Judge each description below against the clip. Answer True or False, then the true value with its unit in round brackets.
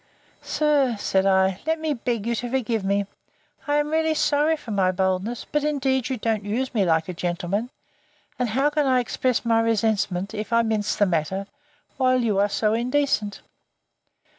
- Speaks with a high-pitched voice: True (230 Hz)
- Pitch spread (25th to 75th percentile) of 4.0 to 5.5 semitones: True (4.8 semitones)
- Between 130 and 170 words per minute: False (180 wpm)